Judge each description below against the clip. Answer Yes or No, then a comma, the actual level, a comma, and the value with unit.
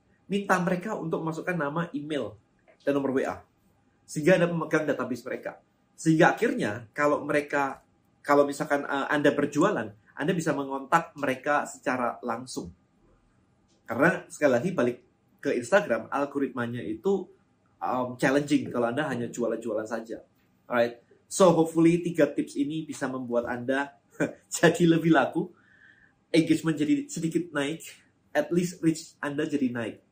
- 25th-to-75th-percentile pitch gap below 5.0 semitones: Yes, average, 3.4 semitones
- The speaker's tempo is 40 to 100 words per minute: No, average, 135 wpm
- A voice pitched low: No, medium, 145 Hz